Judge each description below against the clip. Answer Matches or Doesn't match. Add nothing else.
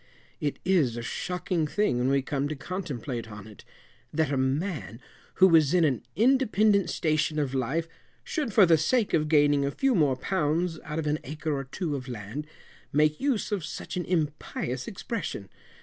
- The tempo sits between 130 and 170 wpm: Doesn't match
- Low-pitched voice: Doesn't match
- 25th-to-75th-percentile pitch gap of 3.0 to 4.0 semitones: Doesn't match